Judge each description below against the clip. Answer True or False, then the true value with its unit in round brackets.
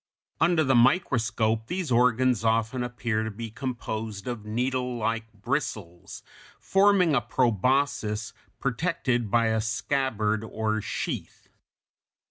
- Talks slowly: True (105 wpm)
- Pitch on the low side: True (115 Hz)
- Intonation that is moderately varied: True (3.0 semitones)